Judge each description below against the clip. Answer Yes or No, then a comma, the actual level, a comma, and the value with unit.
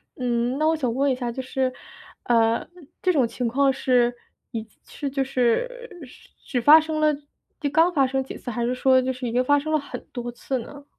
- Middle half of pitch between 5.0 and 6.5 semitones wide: No, average, 2.8 semitones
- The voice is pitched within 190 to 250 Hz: No, very high, 260 Hz